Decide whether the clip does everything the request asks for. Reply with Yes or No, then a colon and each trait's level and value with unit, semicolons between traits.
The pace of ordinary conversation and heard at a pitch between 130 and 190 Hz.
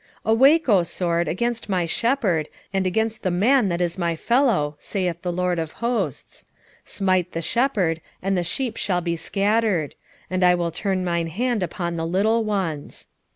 Yes: average, 175 wpm; medium, 185 Hz